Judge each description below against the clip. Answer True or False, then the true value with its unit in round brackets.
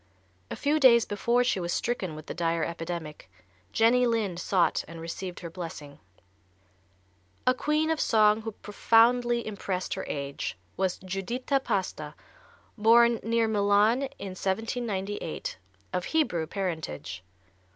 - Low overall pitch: False (205 Hz)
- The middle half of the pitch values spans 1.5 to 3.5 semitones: False (5.3 semitones)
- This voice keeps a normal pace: False (130 wpm)